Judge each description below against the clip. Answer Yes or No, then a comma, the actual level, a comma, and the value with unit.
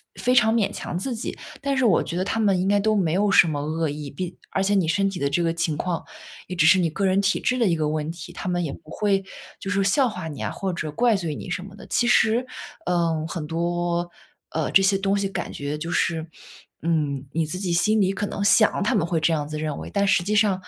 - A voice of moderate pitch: Yes, medium, 180 Hz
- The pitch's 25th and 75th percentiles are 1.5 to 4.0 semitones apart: Yes, average, 3.7 semitones